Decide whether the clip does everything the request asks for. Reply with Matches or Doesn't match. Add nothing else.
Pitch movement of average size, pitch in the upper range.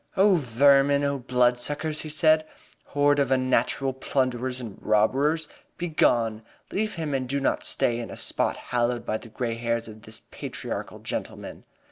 Doesn't match